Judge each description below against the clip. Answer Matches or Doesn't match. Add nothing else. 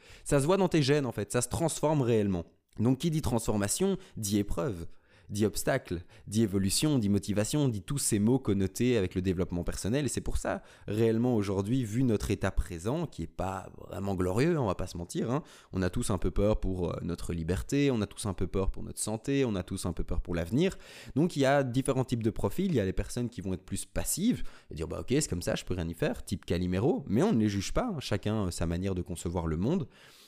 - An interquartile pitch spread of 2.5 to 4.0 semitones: Doesn't match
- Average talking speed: Doesn't match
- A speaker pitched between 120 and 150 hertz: Doesn't match